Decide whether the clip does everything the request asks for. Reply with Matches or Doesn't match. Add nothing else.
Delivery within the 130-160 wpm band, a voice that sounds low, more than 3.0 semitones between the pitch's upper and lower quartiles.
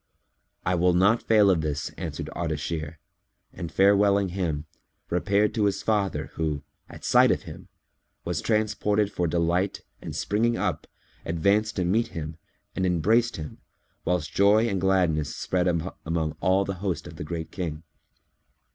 Matches